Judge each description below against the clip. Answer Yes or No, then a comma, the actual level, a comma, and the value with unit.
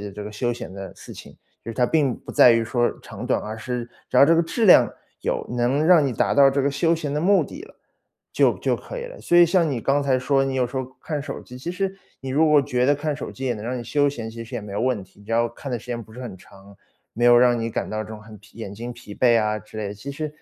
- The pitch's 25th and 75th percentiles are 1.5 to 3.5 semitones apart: No, average, 4.2 semitones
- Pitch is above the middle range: No, low, 125 Hz